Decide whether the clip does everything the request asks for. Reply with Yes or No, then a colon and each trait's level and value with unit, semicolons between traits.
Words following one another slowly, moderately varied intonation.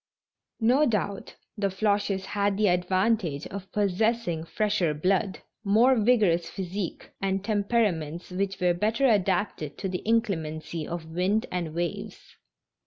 Yes: slow, 125 wpm; average, 3.4 semitones